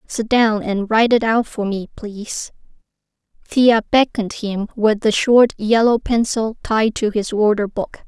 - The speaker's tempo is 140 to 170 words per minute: Yes, average, 165 wpm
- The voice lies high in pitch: Yes, high, 220 Hz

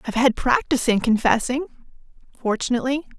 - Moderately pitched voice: No, high, 245 Hz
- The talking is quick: No, slow, 115 wpm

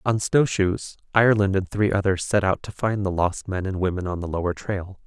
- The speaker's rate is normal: No, fast, 225 wpm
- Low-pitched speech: Yes, very low, 95 Hz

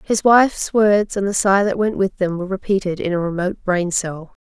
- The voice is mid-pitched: No, high, 195 Hz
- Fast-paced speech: Yes, fast, 230 wpm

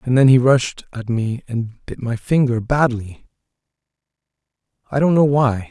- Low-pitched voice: Yes, low, 120 Hz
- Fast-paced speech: No, average, 160 wpm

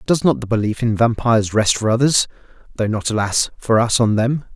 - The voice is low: Yes, low, 115 Hz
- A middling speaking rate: Yes, average, 185 wpm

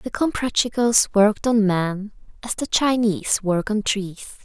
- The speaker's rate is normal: Yes, average, 150 wpm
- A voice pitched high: Yes, high, 215 Hz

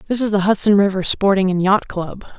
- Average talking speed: No, fast, 225 wpm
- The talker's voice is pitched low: No, high, 195 Hz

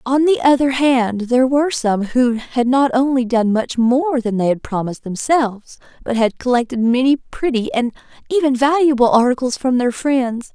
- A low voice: No, very high, 255 Hz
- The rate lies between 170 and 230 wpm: Yes, average, 175 wpm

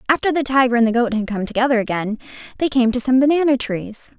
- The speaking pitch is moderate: No, very high, 250 Hz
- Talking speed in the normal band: No, fast, 230 wpm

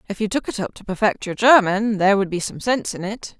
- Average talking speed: No, fast, 285 wpm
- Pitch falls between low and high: No, high, 205 Hz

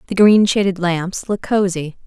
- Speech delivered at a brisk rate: No, average, 175 wpm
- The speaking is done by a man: No, female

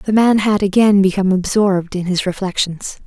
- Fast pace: No, average, 175 wpm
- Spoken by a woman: Yes, female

